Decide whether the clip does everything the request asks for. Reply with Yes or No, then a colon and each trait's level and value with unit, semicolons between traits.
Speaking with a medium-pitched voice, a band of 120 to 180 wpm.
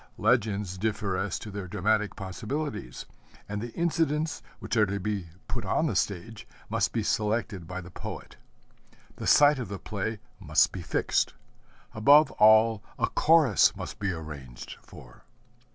No: low, 105 Hz; average, 150 wpm